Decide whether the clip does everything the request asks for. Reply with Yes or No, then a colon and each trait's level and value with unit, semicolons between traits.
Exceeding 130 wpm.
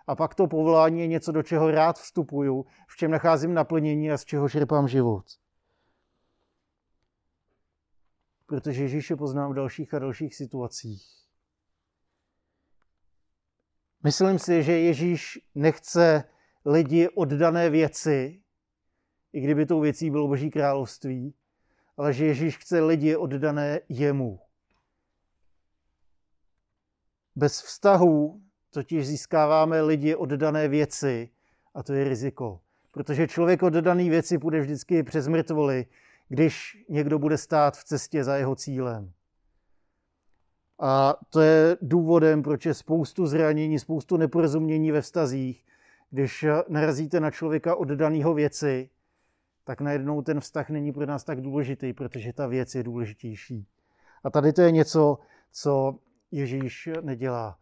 No: average, 125 wpm